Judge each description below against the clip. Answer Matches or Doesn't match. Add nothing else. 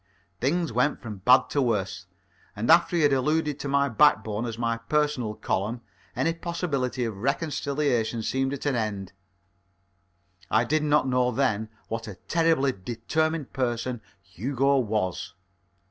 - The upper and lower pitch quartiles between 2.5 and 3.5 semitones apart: Doesn't match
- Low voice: Matches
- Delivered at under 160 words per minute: Matches